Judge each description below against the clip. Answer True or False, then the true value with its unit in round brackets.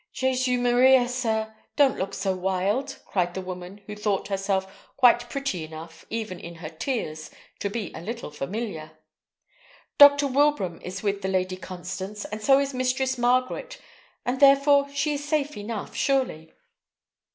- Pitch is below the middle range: False (220 Hz)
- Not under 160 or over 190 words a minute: False (150 wpm)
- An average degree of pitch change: False (6.0 semitones)